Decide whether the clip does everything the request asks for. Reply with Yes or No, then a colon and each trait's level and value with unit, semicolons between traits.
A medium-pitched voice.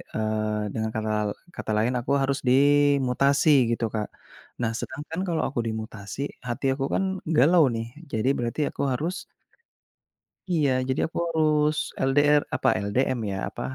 No: low, 130 Hz